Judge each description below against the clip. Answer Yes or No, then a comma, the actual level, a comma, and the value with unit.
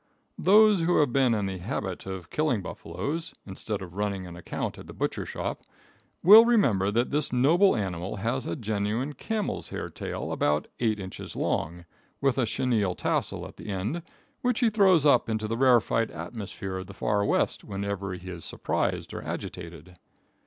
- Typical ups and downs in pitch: No, wide, 7.2 semitones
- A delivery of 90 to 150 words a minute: No, average, 175 wpm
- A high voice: No, low, 110 Hz